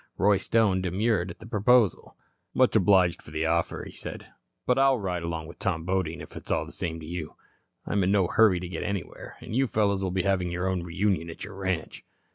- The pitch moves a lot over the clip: No, average, 3.2 semitones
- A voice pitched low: Yes, very low, 95 Hz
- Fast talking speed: Yes, fast, 225 wpm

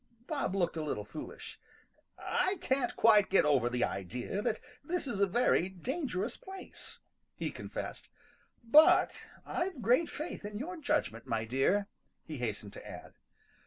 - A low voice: No, high, 205 Hz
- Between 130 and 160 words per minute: Yes, average, 150 wpm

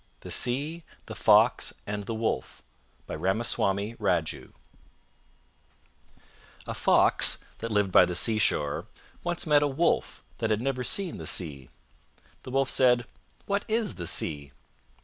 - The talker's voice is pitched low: Yes, low, 115 Hz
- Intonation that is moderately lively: No, wide, 6.4 semitones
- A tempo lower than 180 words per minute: Yes, slow, 135 wpm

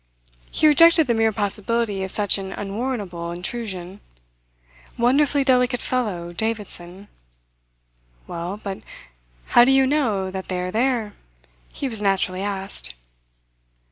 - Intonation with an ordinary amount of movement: Yes, average, 4.5 semitones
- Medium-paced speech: No, slow, 120 wpm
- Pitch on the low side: No, high, 210 Hz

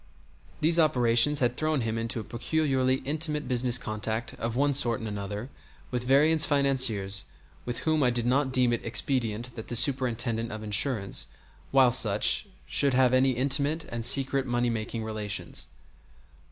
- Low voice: Yes, low, 125 Hz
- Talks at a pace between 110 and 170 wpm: Yes, average, 155 wpm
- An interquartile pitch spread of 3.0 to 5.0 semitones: Yes, average, 3.3 semitones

